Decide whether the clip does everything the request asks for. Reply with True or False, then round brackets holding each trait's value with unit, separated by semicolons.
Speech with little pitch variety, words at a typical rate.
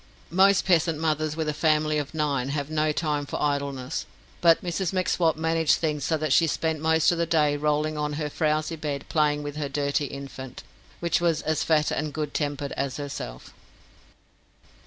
True (1.8 semitones; 180 wpm)